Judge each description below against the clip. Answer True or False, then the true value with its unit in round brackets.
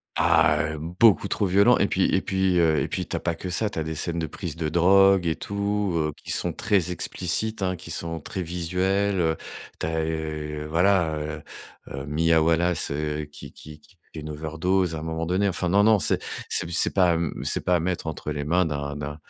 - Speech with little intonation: False (3.1 semitones)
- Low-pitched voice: True (85 Hz)